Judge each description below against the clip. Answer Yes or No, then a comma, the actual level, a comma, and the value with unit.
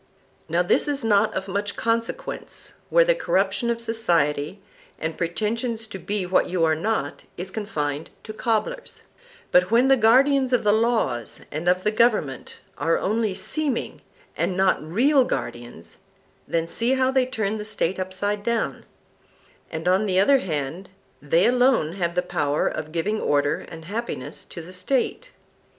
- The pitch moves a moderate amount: No, wide, 5.7 semitones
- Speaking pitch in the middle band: No, high, 200 Hz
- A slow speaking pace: No, average, 160 wpm